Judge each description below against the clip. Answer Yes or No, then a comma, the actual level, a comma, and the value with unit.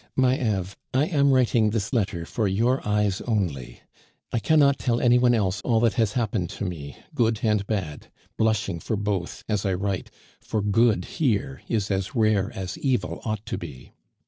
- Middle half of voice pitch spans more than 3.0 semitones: Yes, average, 3.6 semitones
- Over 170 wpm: Yes, average, 180 wpm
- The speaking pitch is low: Yes, low, 105 Hz